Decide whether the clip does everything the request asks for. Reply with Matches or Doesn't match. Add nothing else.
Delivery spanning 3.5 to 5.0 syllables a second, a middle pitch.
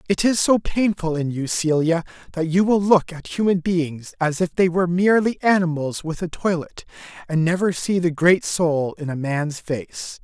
Matches